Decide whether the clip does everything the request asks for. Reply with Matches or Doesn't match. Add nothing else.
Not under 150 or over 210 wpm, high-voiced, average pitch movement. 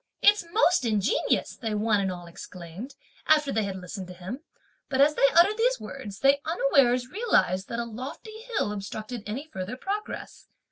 Doesn't match